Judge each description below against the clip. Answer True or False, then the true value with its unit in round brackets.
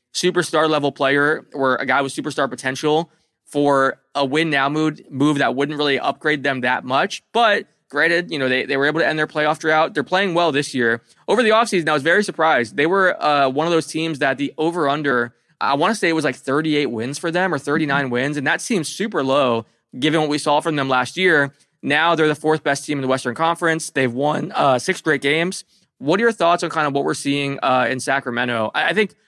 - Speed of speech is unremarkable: False (240 wpm)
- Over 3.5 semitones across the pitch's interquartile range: False (2.8 semitones)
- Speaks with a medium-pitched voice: True (150 Hz)